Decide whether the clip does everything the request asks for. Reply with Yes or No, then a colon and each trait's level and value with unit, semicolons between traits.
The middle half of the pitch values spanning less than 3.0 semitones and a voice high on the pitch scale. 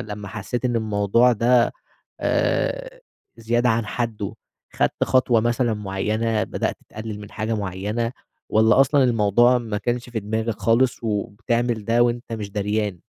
No: narrow, 2.4 semitones; low, 115 Hz